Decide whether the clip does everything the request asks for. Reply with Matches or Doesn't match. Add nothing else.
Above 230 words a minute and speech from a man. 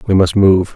Matches